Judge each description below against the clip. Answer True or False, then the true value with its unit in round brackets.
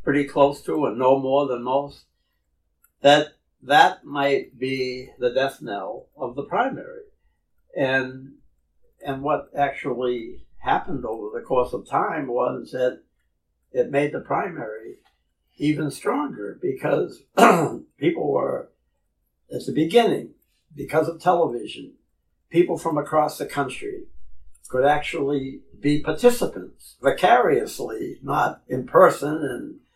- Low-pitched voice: False (145 Hz)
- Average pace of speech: False (120 wpm)